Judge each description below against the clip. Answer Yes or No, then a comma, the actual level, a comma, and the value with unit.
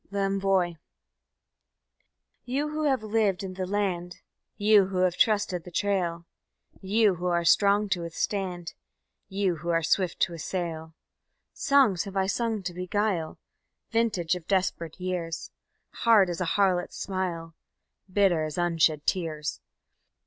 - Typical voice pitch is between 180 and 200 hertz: Yes, medium, 185 Hz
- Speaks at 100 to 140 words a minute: Yes, slow, 135 wpm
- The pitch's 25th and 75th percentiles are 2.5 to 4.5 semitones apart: Yes, average, 2.9 semitones